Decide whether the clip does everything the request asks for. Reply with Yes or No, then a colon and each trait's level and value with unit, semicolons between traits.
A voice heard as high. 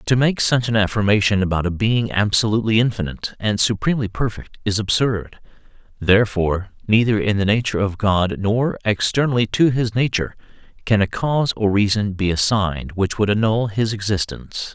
No: low, 105 Hz